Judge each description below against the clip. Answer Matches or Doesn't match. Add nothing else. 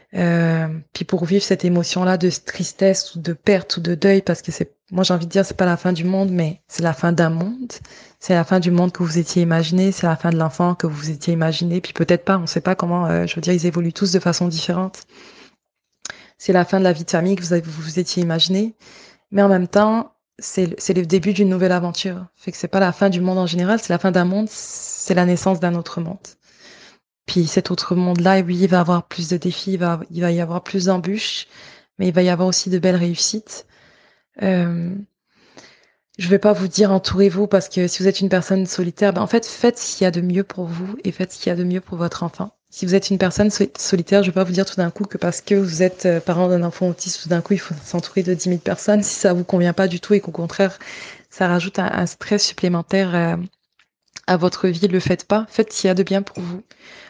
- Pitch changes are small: Matches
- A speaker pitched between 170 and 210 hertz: Matches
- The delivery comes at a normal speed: Doesn't match